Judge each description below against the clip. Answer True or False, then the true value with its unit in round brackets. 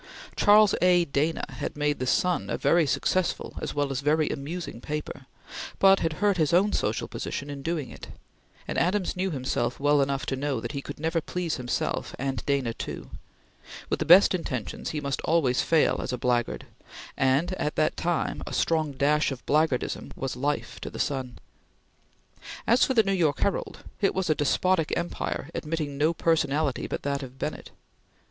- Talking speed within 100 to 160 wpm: False (185 wpm)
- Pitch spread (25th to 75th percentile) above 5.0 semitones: False (3.8 semitones)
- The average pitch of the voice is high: False (150 Hz)